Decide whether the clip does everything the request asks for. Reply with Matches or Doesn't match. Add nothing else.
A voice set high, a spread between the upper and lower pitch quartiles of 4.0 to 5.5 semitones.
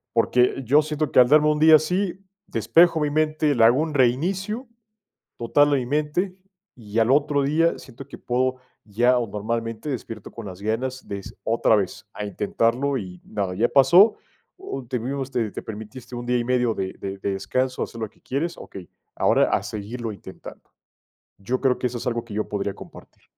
Doesn't match